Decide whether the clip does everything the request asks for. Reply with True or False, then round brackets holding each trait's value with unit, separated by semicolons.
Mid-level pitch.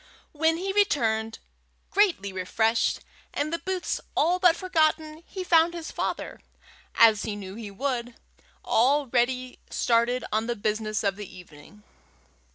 False (245 Hz)